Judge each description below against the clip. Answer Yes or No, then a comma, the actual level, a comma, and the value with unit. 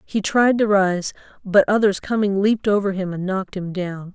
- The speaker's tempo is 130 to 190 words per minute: No, fast, 205 wpm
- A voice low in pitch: No, high, 195 Hz